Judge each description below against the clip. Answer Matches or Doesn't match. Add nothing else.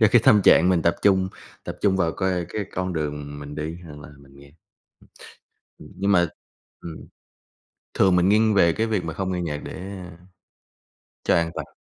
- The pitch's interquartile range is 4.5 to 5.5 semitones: Doesn't match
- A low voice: Matches